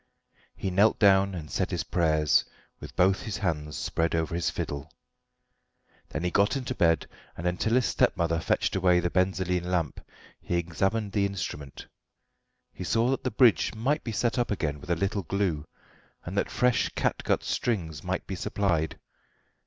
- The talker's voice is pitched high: No, very low, 90 Hz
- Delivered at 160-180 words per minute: Yes, average, 170 wpm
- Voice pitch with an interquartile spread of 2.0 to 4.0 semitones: Yes, average, 3.7 semitones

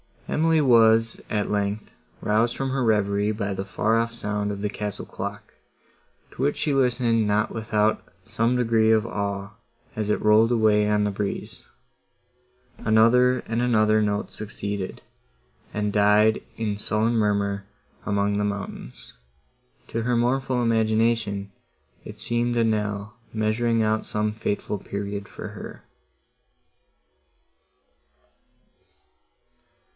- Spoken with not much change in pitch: Yes, narrow, 2.0 semitones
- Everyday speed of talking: No, slow, 120 wpm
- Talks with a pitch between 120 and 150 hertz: No, low, 110 Hz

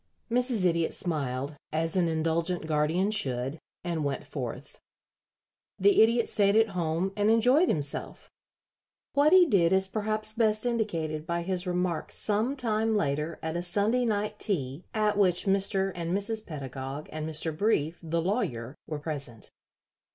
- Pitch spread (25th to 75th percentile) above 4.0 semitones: Yes, wide, 5.4 semitones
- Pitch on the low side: No, medium, 180 Hz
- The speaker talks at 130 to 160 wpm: Yes, average, 150 wpm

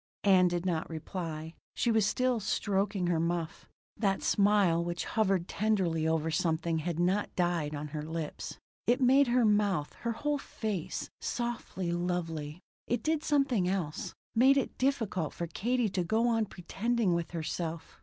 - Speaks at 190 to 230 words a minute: No, average, 155 wpm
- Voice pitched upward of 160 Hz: Yes, medium, 185 Hz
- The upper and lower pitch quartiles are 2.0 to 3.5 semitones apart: No, average, 5.2 semitones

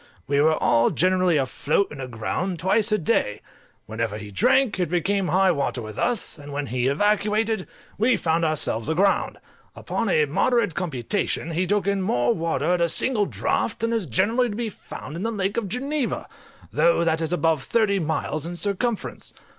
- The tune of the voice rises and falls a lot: Yes, wide, 5.8 semitones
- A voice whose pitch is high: No, medium, 180 Hz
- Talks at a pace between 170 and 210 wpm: Yes, average, 180 wpm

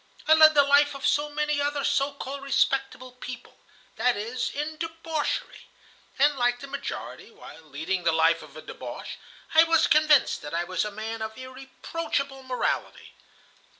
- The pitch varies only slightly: No, average, 4.1 semitones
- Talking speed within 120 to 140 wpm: No, average, 160 wpm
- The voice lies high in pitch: Yes, very high, 275 Hz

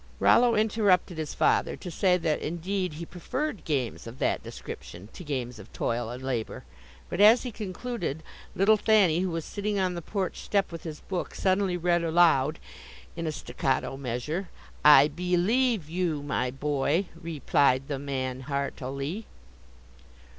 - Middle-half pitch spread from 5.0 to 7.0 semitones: Yes, wide, 5.4 semitones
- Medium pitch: Yes, medium, 165 Hz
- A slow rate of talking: No, average, 165 wpm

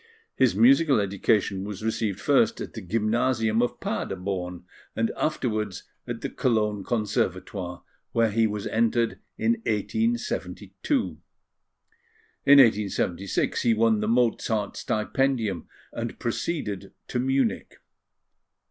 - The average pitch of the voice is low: Yes, low, 110 Hz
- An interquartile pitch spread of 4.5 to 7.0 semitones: No, average, 3.4 semitones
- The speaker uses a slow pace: Yes, slow, 110 wpm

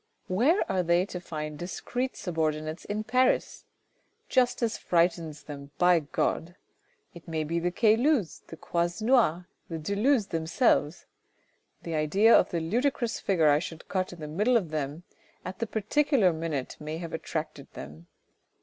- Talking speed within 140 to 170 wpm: Yes, average, 150 wpm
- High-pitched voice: No, medium, 175 Hz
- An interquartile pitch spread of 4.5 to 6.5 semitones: Yes, wide, 5.5 semitones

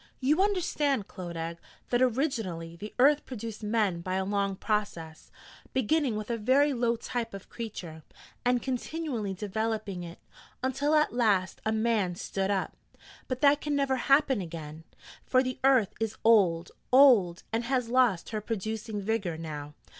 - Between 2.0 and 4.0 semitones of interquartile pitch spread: No, average, 5.3 semitones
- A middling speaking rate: Yes, average, 155 wpm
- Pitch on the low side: No, high, 220 Hz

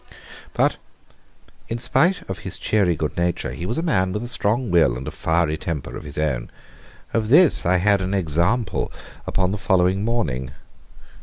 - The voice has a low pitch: Yes, very low, 95 Hz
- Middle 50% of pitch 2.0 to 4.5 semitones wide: No, wide, 5.4 semitones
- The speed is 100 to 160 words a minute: No, average, 175 wpm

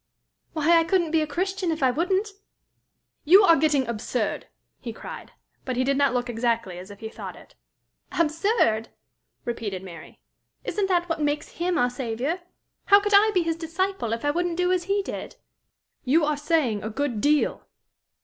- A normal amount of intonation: No, wide, 6.5 semitones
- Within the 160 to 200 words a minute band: Yes, average, 180 wpm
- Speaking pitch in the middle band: No, very high, 300 Hz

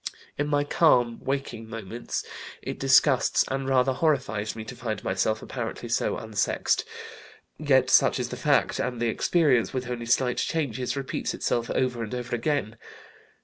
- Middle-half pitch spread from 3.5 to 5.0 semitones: No, average, 2.8 semitones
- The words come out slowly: No, average, 155 wpm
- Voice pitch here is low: Yes, low, 125 Hz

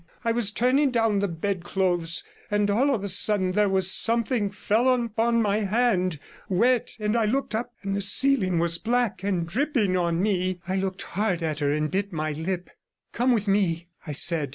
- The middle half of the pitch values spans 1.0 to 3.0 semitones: No, average, 4.3 semitones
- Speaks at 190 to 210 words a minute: Yes, average, 195 wpm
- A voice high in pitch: Yes, high, 200 Hz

